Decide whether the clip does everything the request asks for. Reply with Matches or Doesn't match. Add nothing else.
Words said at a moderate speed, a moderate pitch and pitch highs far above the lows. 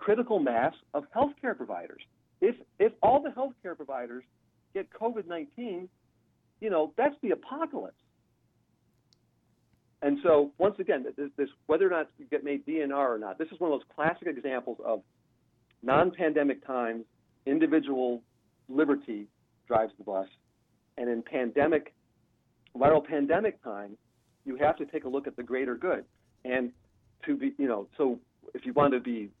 Matches